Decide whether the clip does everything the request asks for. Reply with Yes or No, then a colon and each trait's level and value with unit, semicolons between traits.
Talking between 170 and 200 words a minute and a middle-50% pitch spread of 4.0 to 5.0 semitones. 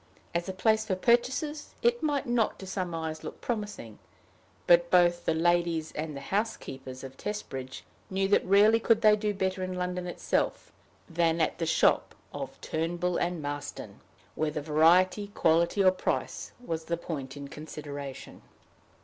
No: average, 160 wpm; average, 4.5 semitones